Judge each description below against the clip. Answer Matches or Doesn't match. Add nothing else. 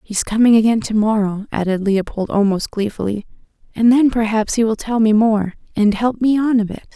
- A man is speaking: Doesn't match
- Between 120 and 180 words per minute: Doesn't match